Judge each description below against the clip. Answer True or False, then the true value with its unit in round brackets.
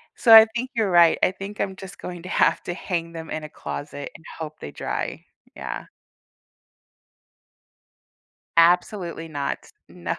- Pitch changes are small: False (3.2 semitones)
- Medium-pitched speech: True (175 Hz)